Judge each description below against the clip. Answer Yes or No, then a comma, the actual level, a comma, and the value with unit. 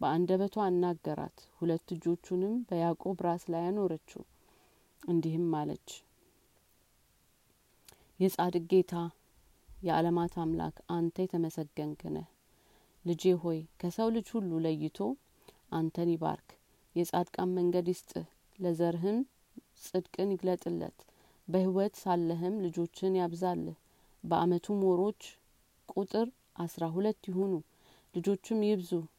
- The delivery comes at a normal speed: Yes, average, 90 wpm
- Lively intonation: No, narrow, 2.0 semitones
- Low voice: No, medium, 175 Hz